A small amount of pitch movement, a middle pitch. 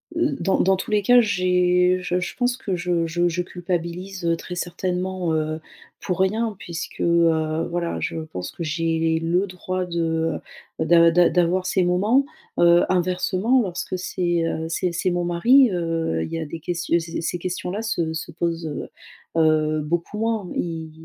Yes: narrow, 2.0 semitones; medium, 175 Hz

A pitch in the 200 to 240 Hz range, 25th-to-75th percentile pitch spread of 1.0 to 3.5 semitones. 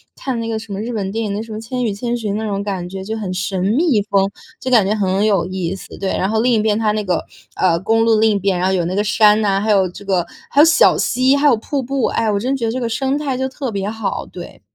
Yes: high, 215 Hz; average, 3.1 semitones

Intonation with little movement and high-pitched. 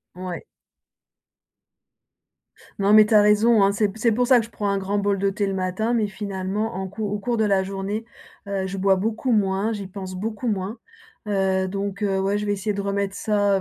Yes: narrow, 1.8 semitones; high, 200 Hz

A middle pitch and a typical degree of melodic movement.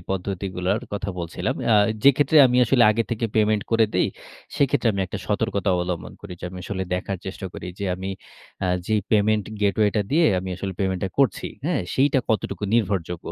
No: low, 105 Hz; average, 3.4 semitones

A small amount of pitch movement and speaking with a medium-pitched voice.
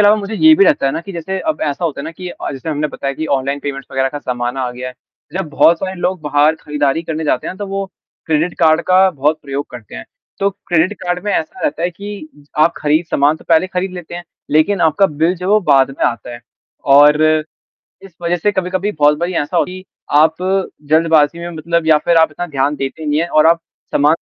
No: average, 3.7 semitones; medium, 160 Hz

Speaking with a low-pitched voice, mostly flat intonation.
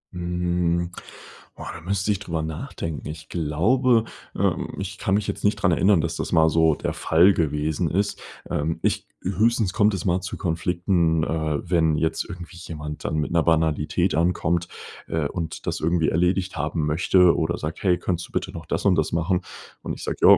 Yes: very low, 85 Hz; narrow, 2.3 semitones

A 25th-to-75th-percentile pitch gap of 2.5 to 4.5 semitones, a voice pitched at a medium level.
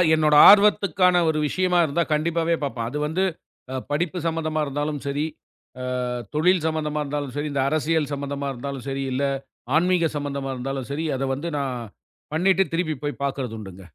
Yes: average, 3.0 semitones; medium, 150 Hz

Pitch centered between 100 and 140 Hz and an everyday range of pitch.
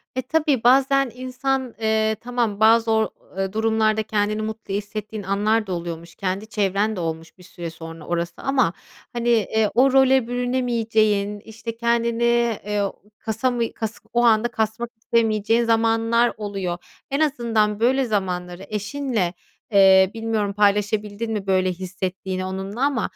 No: high, 220 Hz; average, 3.0 semitones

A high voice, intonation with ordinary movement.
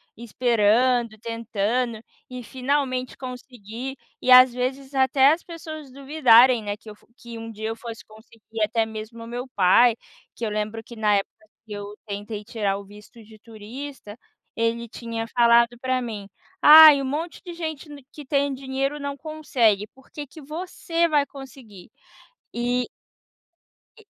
Yes: high, 240 Hz; average, 3.7 semitones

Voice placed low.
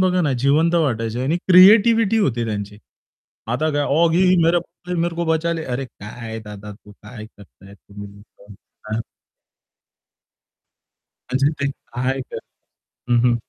Yes: low, 130 Hz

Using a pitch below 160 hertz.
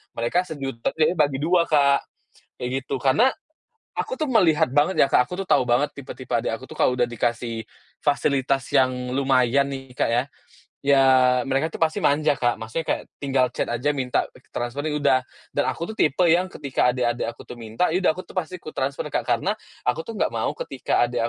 Yes: low, 135 Hz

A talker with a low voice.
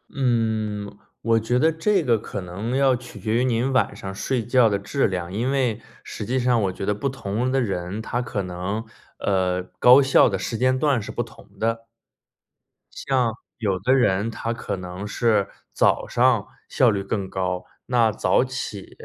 Yes: low, 115 Hz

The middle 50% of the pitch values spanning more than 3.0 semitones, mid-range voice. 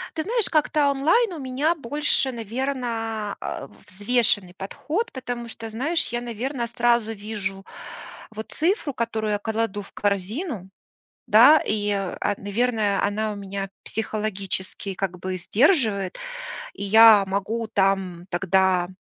No: average, 4.3 semitones; high, 220 Hz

